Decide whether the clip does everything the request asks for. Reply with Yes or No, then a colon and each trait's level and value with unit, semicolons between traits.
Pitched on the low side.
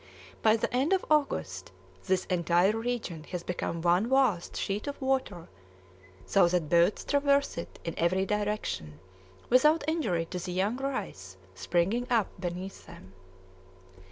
No: high, 195 Hz